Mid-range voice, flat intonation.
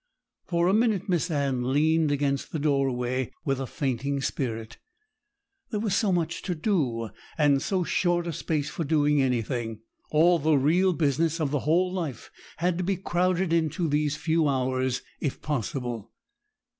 No: medium, 150 Hz; average, 4.3 semitones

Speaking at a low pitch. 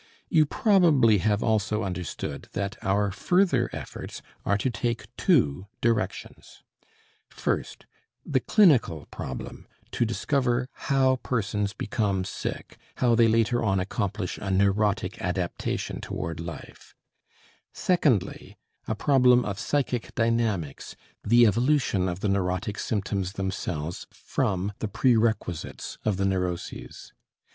Yes: low, 105 Hz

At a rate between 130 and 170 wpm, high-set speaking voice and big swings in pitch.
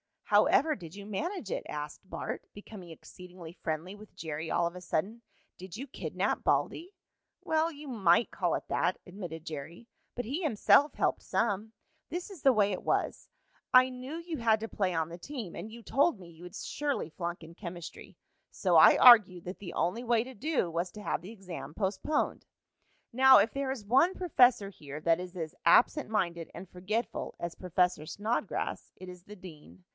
No: average, 190 wpm; high, 200 Hz; wide, 6.3 semitones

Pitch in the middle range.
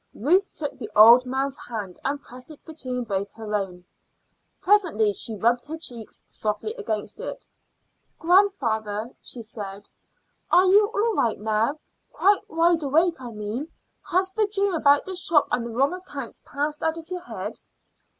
No: very high, 275 Hz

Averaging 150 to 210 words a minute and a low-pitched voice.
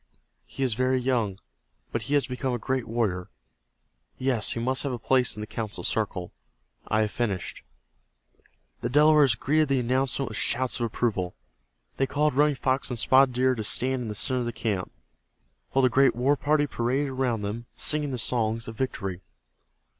Yes: average, 185 wpm; low, 125 Hz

